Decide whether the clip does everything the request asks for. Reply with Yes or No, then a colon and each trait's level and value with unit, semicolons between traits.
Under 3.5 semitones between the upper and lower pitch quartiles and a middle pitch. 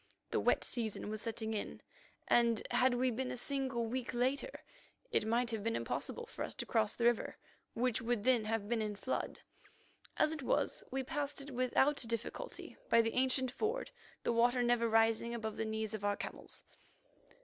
No: narrow, 2.6 semitones; high, 235 Hz